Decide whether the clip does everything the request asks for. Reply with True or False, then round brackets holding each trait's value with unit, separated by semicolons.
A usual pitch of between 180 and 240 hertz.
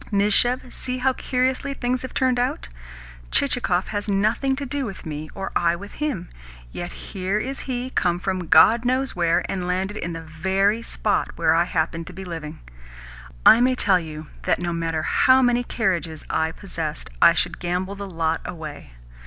True (190 Hz)